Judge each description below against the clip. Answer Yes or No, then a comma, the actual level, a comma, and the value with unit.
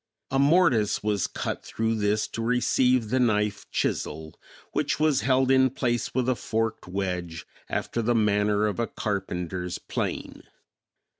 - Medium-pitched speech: No, low, 110 Hz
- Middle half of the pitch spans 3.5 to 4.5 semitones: Yes, average, 3.8 semitones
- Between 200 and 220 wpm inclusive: No, average, 145 wpm